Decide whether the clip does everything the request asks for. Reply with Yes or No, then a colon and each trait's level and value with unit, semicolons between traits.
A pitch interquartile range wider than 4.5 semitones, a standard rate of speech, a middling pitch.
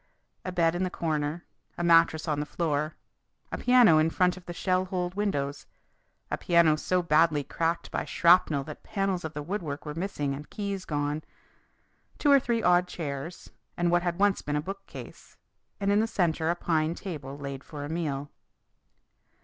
No: average, 3.5 semitones; average, 180 wpm; medium, 170 Hz